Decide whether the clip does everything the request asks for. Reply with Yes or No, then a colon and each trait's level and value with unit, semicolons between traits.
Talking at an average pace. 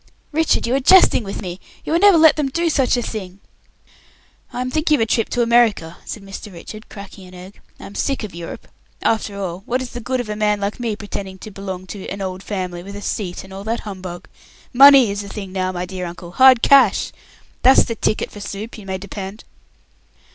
No: fast, 225 wpm